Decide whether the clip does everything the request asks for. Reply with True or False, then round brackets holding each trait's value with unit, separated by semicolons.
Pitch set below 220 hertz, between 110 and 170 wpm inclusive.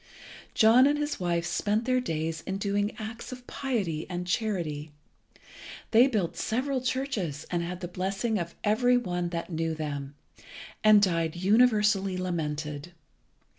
True (190 Hz; 140 wpm)